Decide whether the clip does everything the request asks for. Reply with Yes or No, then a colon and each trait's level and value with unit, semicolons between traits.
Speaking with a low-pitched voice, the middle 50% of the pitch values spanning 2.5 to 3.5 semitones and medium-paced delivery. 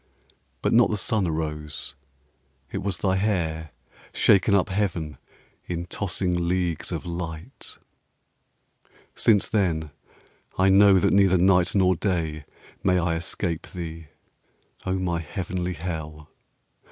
No: very low, 90 Hz; average, 2.8 semitones; slow, 120 wpm